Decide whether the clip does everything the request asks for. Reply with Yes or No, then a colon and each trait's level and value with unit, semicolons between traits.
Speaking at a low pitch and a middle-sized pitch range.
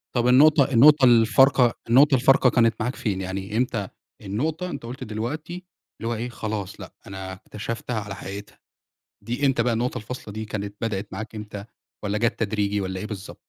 Yes: low, 115 Hz; average, 3.6 semitones